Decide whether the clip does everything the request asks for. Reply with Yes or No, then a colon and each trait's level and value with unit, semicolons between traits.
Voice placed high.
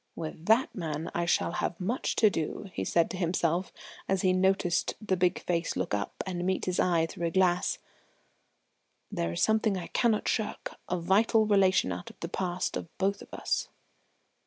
No: medium, 180 Hz